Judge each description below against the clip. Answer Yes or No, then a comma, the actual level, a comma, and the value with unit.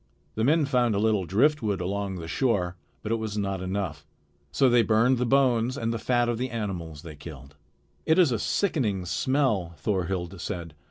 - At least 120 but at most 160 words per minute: No, average, 185 wpm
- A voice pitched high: No, low, 105 Hz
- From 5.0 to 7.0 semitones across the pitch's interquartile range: Yes, average, 5.3 semitones